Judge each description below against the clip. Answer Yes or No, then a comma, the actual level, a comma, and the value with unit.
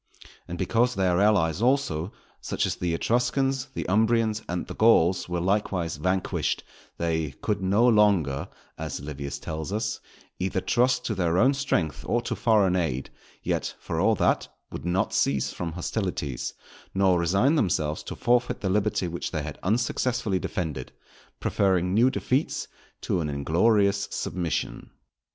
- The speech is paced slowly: No, average, 150 wpm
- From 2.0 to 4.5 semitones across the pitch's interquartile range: No, average, 5.1 semitones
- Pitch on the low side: Yes, very low, 95 Hz